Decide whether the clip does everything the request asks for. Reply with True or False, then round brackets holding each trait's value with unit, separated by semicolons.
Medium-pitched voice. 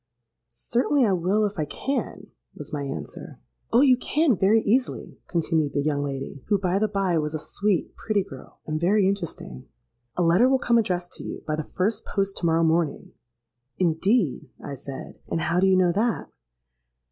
True (180 Hz)